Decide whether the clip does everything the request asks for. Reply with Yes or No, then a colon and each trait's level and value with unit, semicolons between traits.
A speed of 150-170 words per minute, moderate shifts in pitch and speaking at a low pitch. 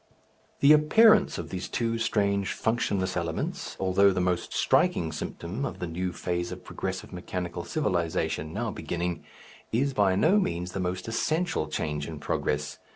Yes: average, 155 wpm; average, 4.9 semitones; very low, 90 Hz